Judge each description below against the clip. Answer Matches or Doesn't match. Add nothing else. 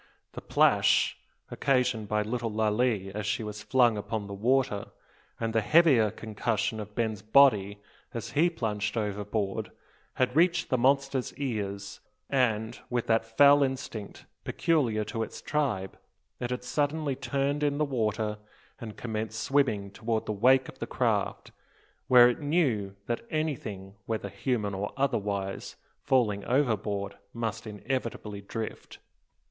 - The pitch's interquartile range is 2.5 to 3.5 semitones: Doesn't match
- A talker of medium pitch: Doesn't match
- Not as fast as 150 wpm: Matches